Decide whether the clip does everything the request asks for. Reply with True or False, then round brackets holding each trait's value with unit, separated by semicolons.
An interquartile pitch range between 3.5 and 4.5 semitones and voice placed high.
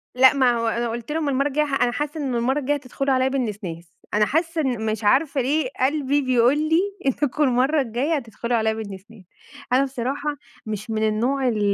True (3.9 semitones; 255 Hz)